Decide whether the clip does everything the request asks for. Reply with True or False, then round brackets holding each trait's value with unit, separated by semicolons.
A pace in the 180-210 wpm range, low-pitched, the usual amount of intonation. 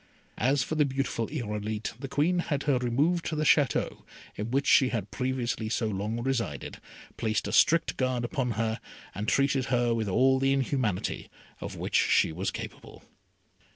False (170 wpm; 125 Hz; 3.7 semitones)